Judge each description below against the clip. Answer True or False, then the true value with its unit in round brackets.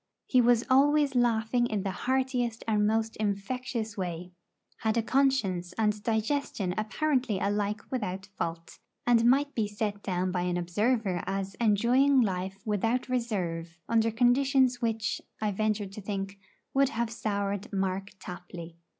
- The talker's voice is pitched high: True (215 Hz)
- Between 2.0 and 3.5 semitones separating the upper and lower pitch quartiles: False (3.9 semitones)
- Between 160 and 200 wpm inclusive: False (140 wpm)